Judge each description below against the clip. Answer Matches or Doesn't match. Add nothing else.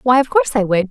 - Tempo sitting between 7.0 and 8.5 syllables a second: Matches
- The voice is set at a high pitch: Matches